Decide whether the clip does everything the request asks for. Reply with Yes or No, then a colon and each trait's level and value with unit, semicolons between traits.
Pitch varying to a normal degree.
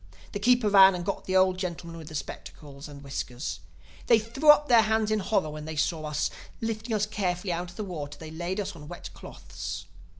No: wide, 5.7 semitones